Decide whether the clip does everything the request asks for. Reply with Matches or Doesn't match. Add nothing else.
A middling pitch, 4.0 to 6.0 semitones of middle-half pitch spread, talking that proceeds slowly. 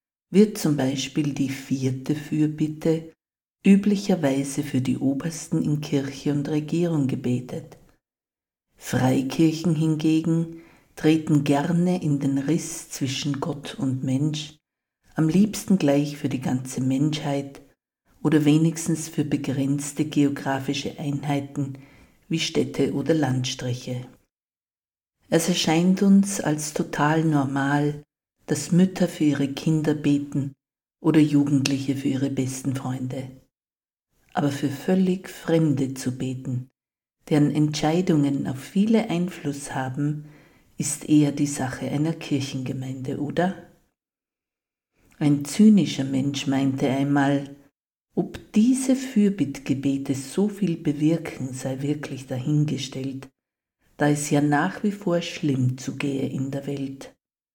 Doesn't match